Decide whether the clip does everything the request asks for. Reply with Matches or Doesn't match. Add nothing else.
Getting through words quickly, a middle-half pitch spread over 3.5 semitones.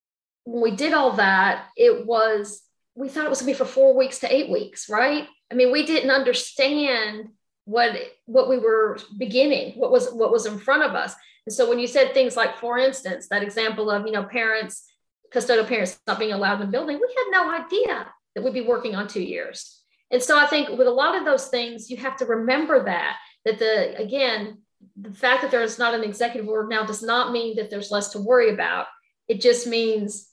Matches